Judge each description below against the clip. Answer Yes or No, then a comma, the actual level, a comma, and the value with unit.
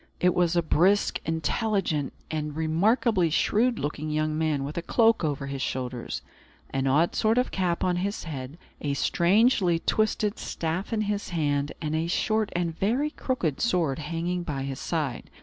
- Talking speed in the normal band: Yes, average, 165 wpm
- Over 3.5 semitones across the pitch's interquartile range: Yes, average, 5.1 semitones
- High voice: No, medium, 170 Hz